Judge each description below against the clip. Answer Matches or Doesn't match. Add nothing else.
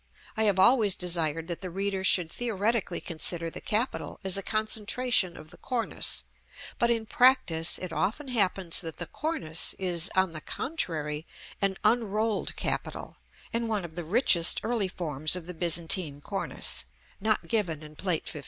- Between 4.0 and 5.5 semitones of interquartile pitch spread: Matches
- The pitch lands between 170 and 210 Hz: Matches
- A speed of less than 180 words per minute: Matches